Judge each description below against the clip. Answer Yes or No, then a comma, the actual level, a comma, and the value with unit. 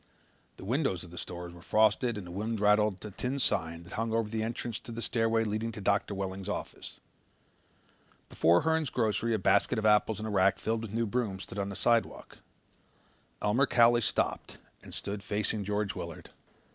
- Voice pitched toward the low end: Yes, low, 105 Hz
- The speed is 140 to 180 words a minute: No, average, 190 wpm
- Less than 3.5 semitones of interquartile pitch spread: Yes, average, 2.7 semitones